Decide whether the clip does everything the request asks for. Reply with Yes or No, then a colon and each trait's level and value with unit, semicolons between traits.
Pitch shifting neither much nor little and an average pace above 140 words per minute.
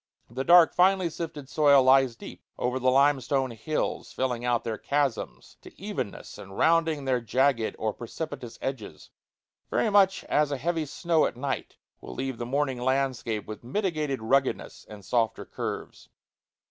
Yes: average, 4.1 semitones; average, 155 wpm